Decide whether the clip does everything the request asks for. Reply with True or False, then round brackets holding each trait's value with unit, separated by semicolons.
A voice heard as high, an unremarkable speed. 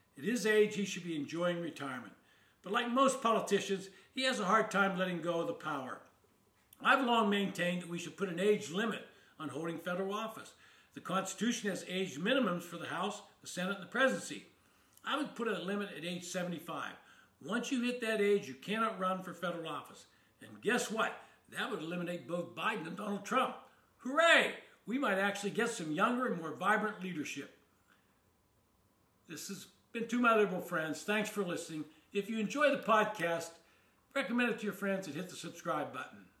True (195 Hz; 190 wpm)